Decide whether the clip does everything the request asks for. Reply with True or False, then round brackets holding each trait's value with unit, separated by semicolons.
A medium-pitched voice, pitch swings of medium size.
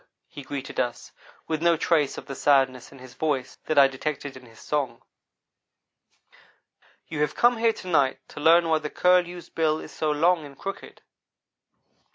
True (150 Hz; 3.6 semitones)